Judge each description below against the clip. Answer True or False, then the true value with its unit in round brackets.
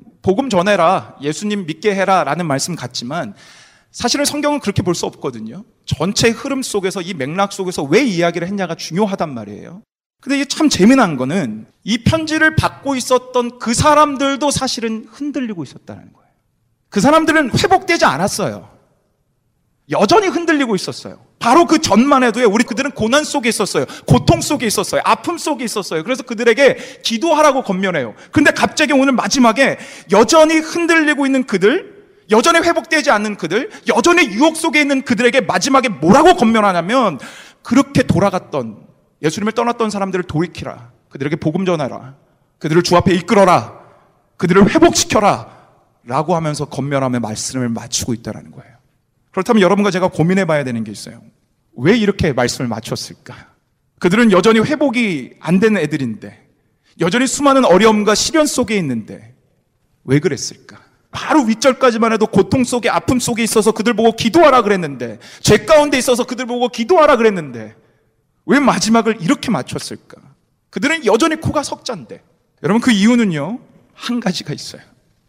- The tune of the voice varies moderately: False (7.9 semitones)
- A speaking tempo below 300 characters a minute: False (370 characters per minute)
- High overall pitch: True (220 Hz)